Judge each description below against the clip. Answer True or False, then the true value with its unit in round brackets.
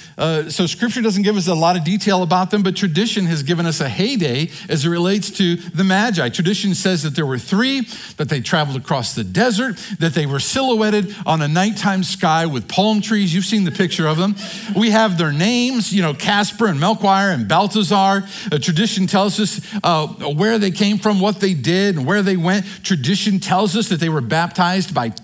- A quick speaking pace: True (210 wpm)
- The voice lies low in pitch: False (190 Hz)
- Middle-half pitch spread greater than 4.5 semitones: False (3.6 semitones)